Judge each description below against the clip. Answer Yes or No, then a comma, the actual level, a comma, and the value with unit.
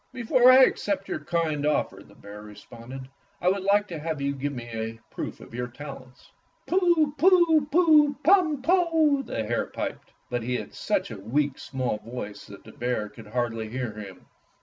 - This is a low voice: No, medium, 145 Hz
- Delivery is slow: No, average, 185 wpm